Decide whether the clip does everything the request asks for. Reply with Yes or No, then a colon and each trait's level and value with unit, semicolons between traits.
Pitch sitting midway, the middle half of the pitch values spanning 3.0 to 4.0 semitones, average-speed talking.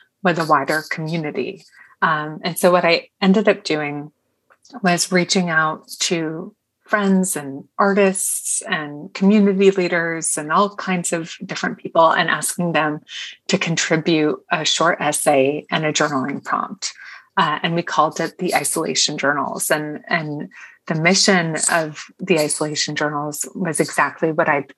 Yes: medium, 165 Hz; average, 3.3 semitones; average, 145 wpm